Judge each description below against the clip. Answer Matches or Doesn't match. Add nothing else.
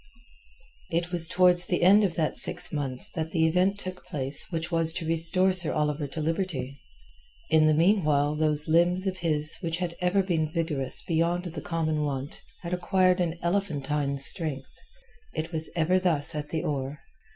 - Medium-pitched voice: Matches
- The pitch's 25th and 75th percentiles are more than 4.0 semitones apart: Doesn't match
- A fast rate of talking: Doesn't match